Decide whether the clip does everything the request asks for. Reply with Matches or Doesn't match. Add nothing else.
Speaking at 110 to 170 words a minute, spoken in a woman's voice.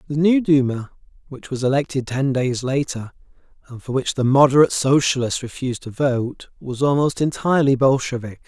Doesn't match